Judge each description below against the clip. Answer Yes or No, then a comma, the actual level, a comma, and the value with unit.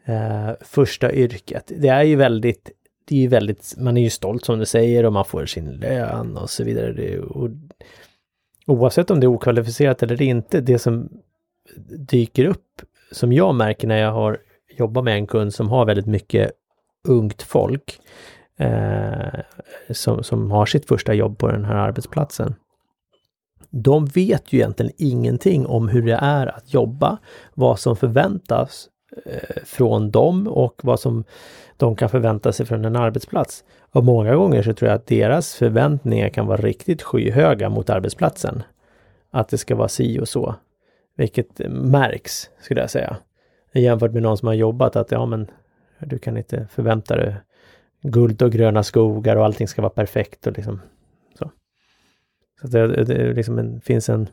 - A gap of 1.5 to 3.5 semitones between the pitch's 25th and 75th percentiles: Yes, average, 3.0 semitones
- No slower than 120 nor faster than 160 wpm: No, average, 170 wpm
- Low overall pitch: Yes, low, 115 Hz